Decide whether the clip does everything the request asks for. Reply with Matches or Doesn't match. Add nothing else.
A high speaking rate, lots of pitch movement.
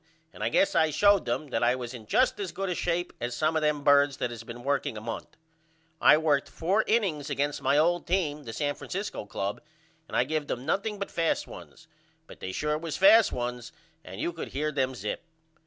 Matches